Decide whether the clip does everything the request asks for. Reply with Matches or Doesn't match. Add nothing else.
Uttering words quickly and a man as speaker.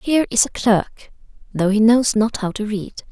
Doesn't match